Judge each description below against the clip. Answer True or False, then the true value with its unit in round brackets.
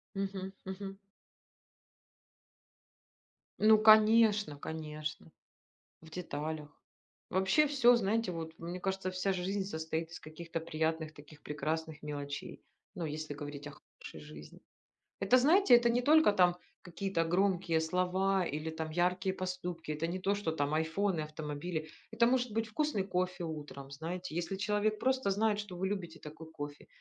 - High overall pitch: False (180 Hz)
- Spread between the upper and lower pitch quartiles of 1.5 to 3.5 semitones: False (4.2 semitones)